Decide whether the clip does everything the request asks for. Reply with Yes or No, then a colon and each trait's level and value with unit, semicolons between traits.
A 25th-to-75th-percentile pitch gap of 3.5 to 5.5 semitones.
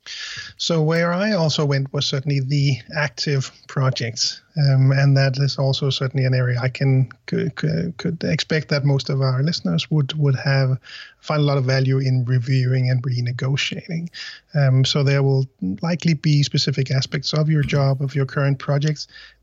No: narrow, 2.4 semitones